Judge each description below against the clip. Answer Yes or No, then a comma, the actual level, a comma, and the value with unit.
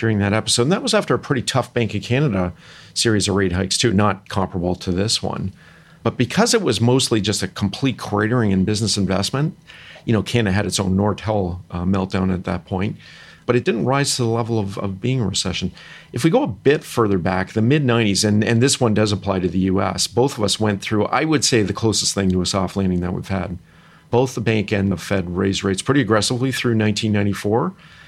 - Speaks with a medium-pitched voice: No, low, 105 Hz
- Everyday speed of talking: No, fast, 230 wpm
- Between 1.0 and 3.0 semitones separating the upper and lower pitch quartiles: No, average, 4.2 semitones